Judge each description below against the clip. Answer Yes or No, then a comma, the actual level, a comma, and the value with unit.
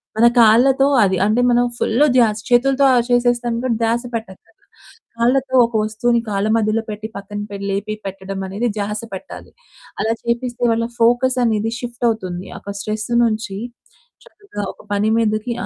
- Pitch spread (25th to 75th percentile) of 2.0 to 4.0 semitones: Yes, narrow, 2.6 semitones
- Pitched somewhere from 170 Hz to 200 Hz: No, high, 225 Hz